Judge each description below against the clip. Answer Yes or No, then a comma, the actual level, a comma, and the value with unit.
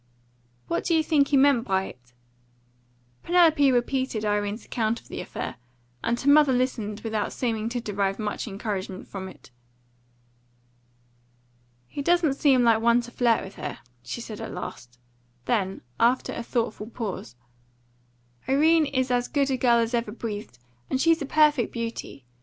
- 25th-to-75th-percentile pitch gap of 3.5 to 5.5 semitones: Yes, average, 4.5 semitones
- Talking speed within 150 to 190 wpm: Yes, average, 160 wpm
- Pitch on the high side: Yes, high, 235 Hz